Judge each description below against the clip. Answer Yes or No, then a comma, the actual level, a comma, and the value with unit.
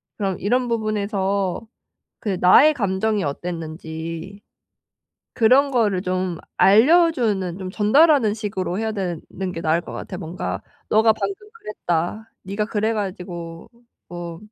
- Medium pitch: No, high, 200 Hz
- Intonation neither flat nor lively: Yes, average, 3.8 semitones